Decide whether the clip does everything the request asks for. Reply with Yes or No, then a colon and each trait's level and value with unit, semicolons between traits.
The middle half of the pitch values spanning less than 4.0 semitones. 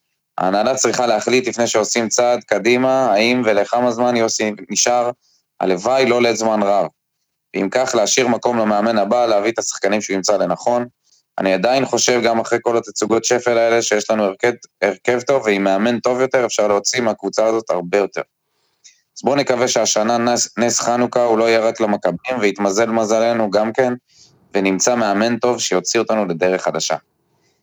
Yes: narrow, 2.6 semitones